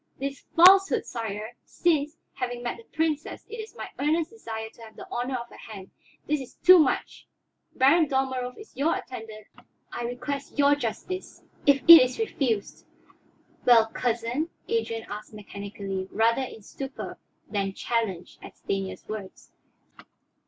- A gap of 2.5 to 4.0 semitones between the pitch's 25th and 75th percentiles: No, average, 4.8 semitones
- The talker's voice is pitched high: Yes, high, 245 Hz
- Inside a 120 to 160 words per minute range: Yes, average, 150 wpm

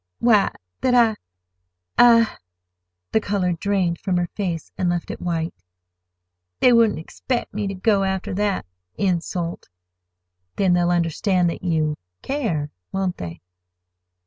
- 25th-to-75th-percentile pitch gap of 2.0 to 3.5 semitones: No, average, 4.0 semitones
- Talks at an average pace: No, slow, 120 wpm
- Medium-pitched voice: Yes, medium, 180 Hz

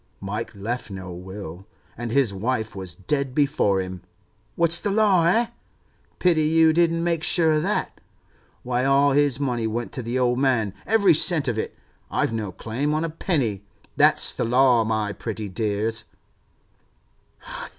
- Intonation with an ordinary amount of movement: No, wide, 6.4 semitones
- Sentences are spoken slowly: No, average, 160 wpm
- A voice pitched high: No, low, 125 Hz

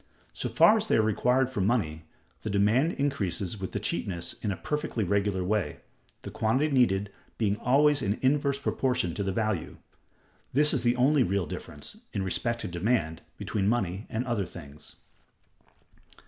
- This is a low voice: Yes, low, 110 Hz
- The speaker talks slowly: No, average, 165 wpm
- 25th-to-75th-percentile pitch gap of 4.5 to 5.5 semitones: Yes, average, 5.2 semitones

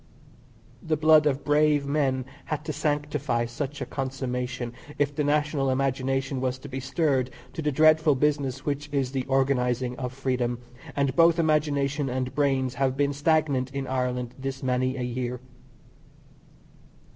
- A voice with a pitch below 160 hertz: Yes, low, 135 Hz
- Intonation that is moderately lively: No, narrow, 2.3 semitones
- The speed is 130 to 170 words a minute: Yes, average, 150 wpm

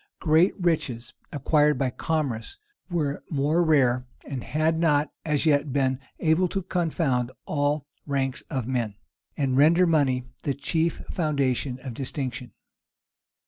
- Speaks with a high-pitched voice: No, medium, 145 Hz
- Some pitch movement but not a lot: Yes, average, 3.5 semitones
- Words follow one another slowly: Yes, slow, 130 wpm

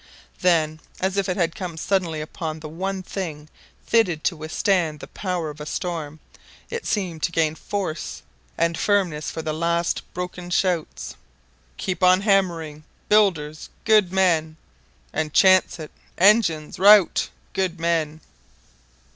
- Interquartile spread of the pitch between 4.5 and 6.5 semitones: No, average, 3.2 semitones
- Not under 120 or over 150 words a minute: Yes, average, 140 wpm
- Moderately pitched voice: Yes, medium, 170 Hz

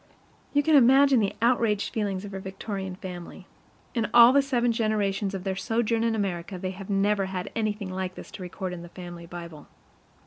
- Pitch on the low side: No, high, 200 Hz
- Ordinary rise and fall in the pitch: Yes, average, 3.5 semitones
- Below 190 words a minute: No, average, 195 wpm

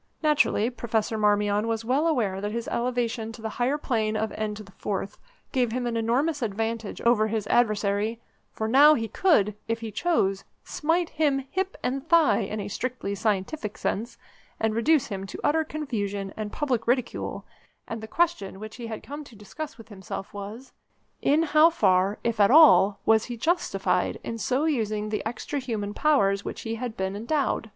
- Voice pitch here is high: Yes, high, 225 Hz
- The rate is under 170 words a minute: No, average, 180 wpm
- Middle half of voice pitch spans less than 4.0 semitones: No, average, 4.4 semitones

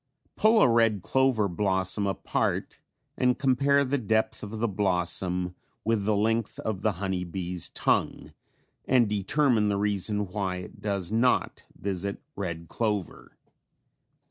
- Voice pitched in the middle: No, low, 105 Hz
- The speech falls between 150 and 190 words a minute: No, slow, 135 wpm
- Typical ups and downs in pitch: Yes, average, 3.4 semitones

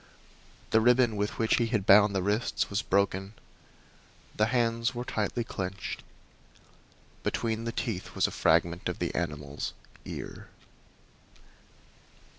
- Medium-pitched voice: No, low, 105 Hz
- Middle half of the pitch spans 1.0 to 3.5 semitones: Yes, average, 3.2 semitones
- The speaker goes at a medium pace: No, slow, 125 wpm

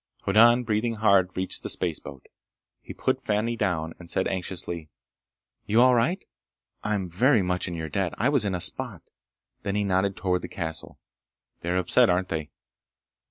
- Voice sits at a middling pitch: No, very low, 95 Hz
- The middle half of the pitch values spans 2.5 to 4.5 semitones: Yes, average, 3.7 semitones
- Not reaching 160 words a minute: No, average, 170 wpm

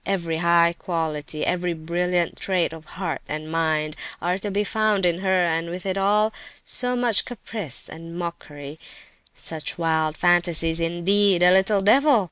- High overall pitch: No, medium, 175 Hz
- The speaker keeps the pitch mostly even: No, average, 3.1 semitones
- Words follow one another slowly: No, average, 150 wpm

